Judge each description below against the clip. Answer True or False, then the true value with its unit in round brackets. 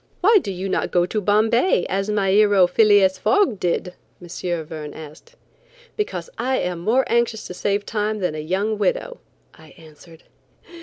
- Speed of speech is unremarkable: True (165 wpm)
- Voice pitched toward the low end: False (195 Hz)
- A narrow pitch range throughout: False (3.9 semitones)